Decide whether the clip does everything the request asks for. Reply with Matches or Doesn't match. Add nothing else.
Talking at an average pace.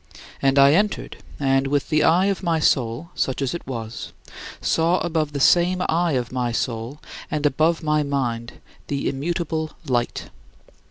Matches